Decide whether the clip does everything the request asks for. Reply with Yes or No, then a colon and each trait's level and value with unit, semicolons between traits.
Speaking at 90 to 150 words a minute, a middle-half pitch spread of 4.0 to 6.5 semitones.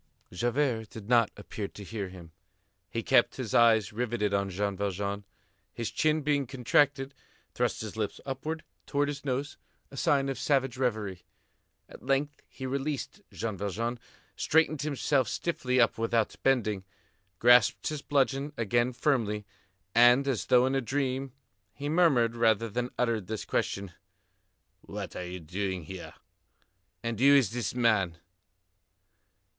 Yes: average, 145 wpm; average, 4.7 semitones